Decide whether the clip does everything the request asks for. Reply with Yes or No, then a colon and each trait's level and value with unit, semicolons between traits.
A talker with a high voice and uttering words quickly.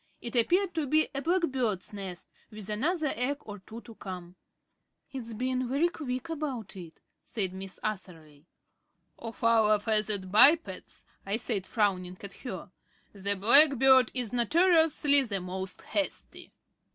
No: high, 230 Hz; average, 140 wpm